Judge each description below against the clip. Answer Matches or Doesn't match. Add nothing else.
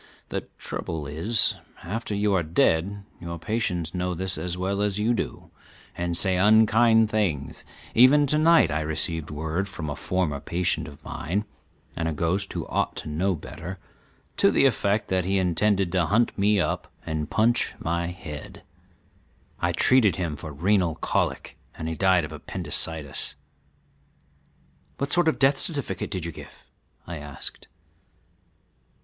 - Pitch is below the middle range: Matches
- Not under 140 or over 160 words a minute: Matches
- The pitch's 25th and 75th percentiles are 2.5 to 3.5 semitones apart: Doesn't match